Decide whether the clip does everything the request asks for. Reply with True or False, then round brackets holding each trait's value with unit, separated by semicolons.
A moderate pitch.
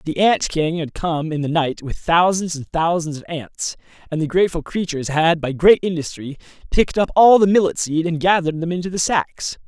True (165 Hz)